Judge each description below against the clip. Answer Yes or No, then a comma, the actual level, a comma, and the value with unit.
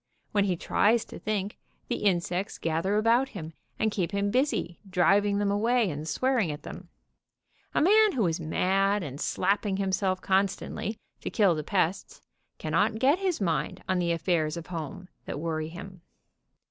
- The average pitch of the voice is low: No, high, 195 Hz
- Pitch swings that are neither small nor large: Yes, average, 3.8 semitones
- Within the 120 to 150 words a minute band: No, average, 165 wpm